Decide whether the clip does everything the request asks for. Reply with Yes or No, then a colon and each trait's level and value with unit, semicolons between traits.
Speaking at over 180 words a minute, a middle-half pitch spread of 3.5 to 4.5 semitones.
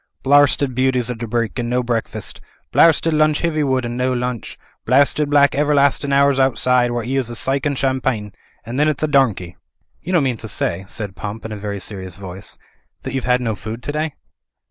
Yes: average, 200 wpm; average, 4.0 semitones